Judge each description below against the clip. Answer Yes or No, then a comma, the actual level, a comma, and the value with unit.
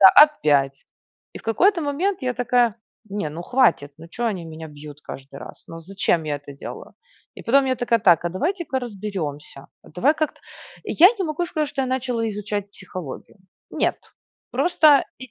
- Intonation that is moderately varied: No, wide, 8.9 semitones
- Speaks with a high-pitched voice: Yes, high, 215 Hz